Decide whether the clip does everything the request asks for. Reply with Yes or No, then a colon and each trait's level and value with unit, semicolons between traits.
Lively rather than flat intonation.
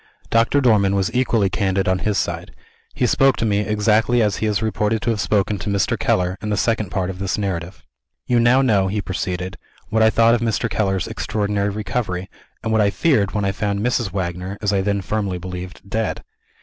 No: narrow, 2.6 semitones